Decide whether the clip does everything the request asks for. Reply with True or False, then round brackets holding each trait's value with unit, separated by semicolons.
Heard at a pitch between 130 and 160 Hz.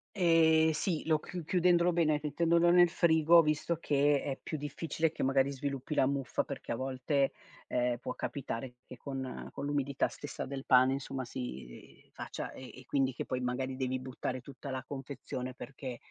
True (140 Hz)